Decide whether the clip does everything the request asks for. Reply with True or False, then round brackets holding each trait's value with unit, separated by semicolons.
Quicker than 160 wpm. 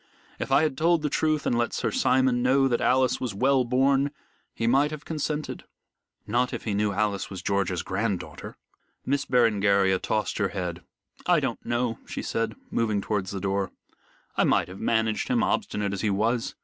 True (190 wpm)